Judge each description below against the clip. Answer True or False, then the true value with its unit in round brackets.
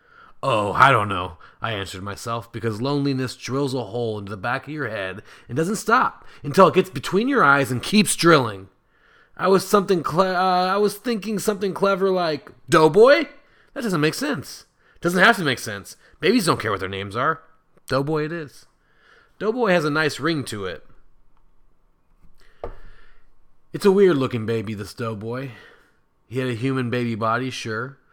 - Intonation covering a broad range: True (8.1 semitones)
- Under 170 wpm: False (175 wpm)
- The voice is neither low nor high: True (145 Hz)